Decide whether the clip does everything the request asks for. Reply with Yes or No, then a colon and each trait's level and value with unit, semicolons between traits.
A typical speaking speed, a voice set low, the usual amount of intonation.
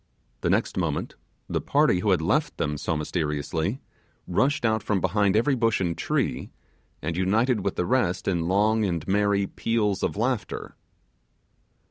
Yes: average, 155 wpm; low, 100 Hz; average, 4.1 semitones